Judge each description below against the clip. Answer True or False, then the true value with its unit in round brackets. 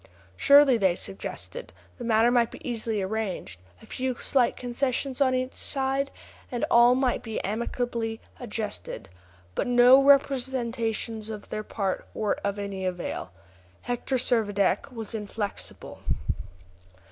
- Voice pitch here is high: True (235 Hz)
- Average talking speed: False (125 wpm)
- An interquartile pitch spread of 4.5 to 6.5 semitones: False (3.2 semitones)